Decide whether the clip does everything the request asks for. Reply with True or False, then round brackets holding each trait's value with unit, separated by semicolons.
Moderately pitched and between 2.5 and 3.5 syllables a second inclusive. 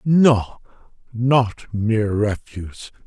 False (115 Hz; 3.1 syllables/s)